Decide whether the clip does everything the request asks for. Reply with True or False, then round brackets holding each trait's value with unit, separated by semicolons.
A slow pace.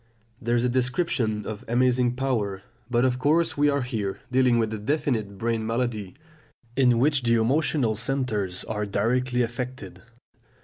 False (150 wpm)